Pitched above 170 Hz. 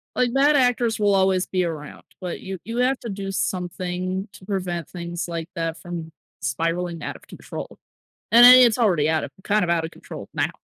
Yes: medium, 185 Hz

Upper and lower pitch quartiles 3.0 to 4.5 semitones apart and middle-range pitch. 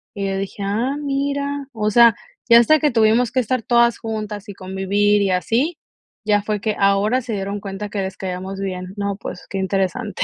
No: average, 3.3 semitones; high, 210 Hz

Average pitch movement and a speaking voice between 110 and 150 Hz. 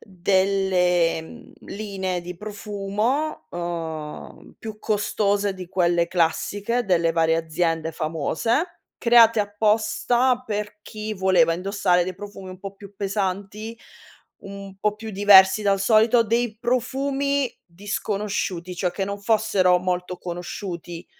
No: average, 3.3 semitones; high, 195 Hz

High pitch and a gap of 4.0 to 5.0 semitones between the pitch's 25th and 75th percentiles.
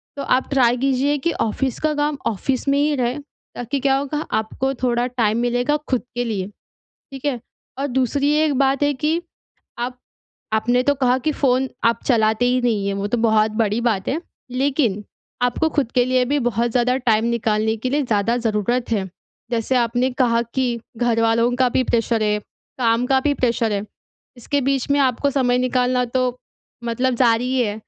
No: high, 245 Hz; average, 2.7 semitones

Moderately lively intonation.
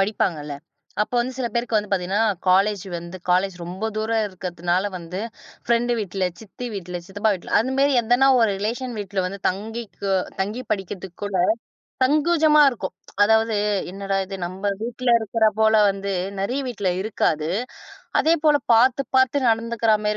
Yes: average, 3.8 semitones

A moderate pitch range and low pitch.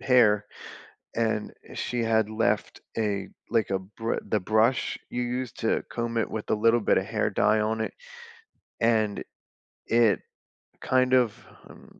No: narrow, 1.7 semitones; low, 110 Hz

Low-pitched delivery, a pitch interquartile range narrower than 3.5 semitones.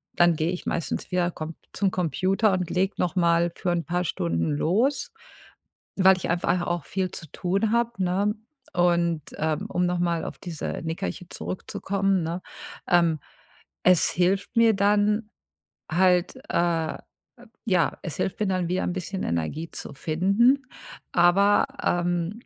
No: medium, 180 Hz; narrow, 2.4 semitones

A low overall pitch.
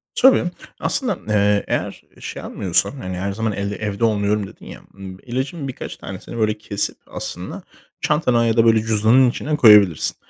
Yes: low, 110 Hz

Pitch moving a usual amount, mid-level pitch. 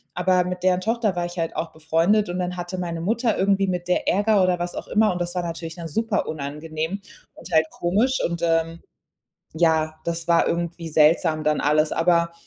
No: narrow, 2.1 semitones; medium, 175 Hz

